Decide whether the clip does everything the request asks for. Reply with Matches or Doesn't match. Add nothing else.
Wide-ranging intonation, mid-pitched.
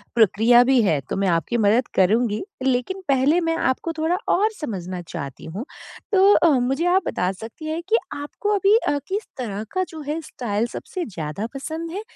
Doesn't match